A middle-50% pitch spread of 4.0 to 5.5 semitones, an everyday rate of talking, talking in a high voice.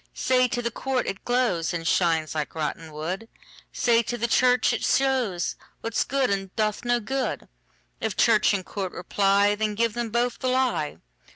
Yes: average, 4.6 semitones; average, 155 wpm; high, 220 Hz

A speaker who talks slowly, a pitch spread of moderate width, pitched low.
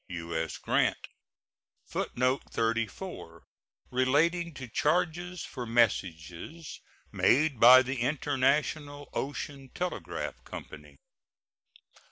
Yes: slow, 80 wpm; average, 4.9 semitones; low, 130 Hz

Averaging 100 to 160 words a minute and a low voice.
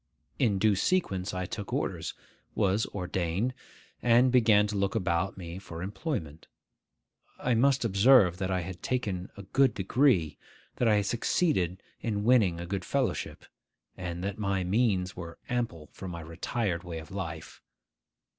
Yes: average, 155 wpm; very low, 95 Hz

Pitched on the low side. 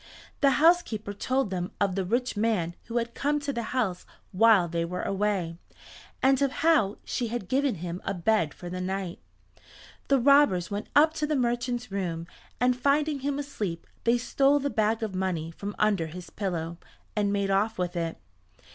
No: high, 210 Hz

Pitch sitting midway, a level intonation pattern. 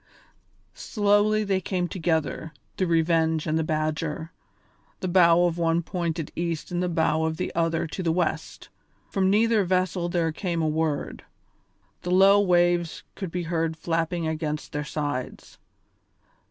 Yes: medium, 170 Hz; narrow, 2.1 semitones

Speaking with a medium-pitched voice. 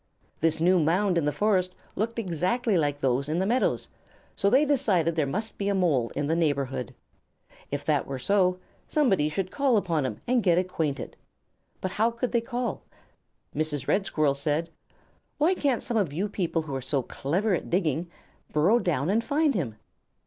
Yes: medium, 180 Hz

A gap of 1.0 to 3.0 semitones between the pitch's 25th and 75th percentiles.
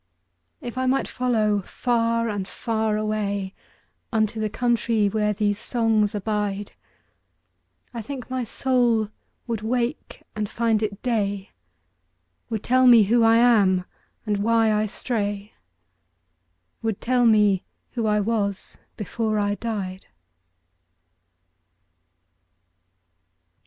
Yes: narrow, 2.5 semitones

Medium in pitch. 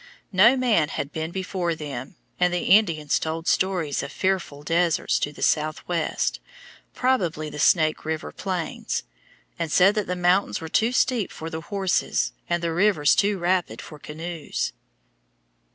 Yes: medium, 170 Hz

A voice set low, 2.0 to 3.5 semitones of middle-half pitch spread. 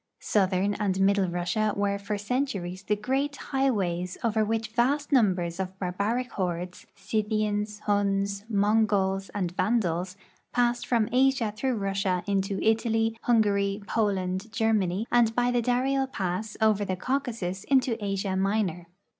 No: high, 205 Hz; average, 3.0 semitones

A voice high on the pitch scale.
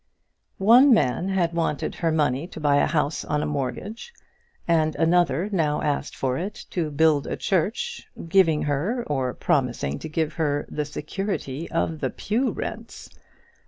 No: medium, 160 Hz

